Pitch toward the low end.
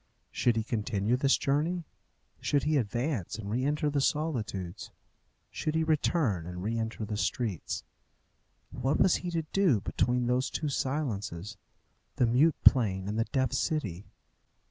Yes: low, 125 Hz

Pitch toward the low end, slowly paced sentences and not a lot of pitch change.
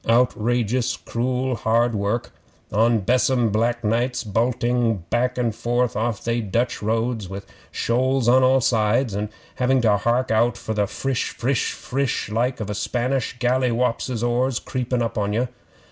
No: low, 120 Hz; average, 155 wpm; narrow, 2.1 semitones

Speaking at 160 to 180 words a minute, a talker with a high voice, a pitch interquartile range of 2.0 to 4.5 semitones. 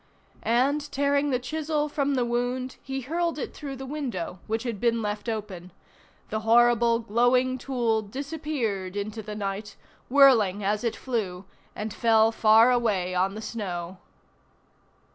No: average, 145 wpm; high, 235 Hz; average, 4.2 semitones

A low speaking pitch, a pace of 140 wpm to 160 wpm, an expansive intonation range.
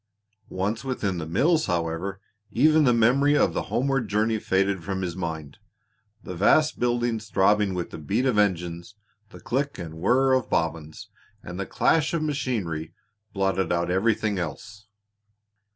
Yes: low, 100 Hz; average, 150 wpm; wide, 5.8 semitones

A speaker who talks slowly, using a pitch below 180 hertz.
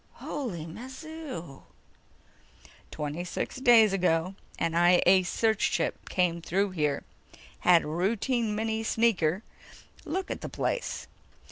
No: slow, 120 wpm; high, 190 Hz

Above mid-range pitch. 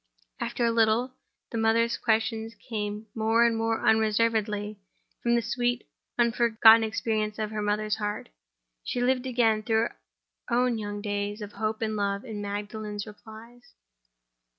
Yes: high, 220 Hz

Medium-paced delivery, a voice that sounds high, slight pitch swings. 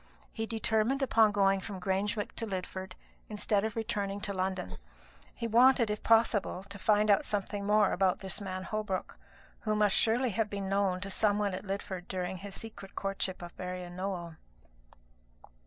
Yes: average, 170 wpm; high, 200 Hz; narrow, 2.2 semitones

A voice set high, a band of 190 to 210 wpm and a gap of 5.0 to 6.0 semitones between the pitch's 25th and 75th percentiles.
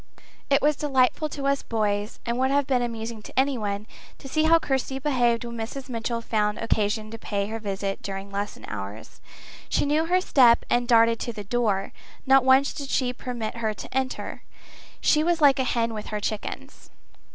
No: high, 235 Hz; average, 195 wpm; average, 3.9 semitones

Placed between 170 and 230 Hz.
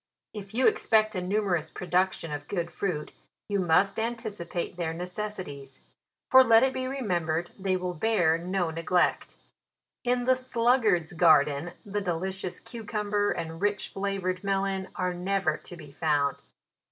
Yes: medium, 185 Hz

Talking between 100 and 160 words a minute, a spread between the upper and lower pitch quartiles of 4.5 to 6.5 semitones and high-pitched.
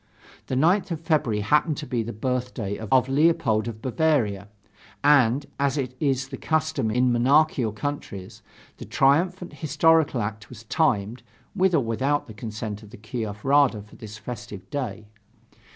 No: average, 150 wpm; average, 5.2 semitones; low, 125 Hz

